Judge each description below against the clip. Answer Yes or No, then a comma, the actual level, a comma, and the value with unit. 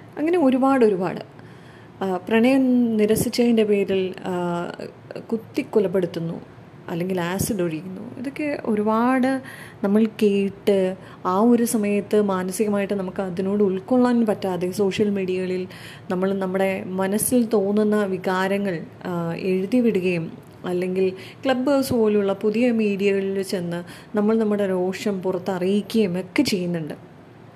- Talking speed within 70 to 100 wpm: Yes, average, 95 wpm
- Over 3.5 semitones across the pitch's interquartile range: No, average, 3.0 semitones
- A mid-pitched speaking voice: No, high, 200 Hz